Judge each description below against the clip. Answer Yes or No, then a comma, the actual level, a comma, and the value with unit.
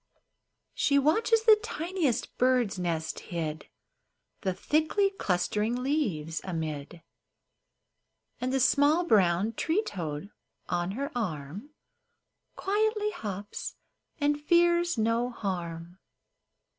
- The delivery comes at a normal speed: No, slow, 95 wpm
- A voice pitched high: Yes, high, 230 Hz